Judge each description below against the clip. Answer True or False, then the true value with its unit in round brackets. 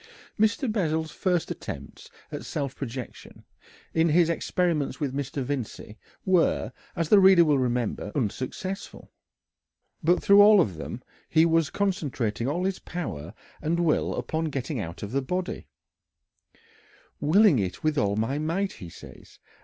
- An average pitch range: False (5.8 semitones)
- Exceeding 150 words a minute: False (145 wpm)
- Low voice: False (155 Hz)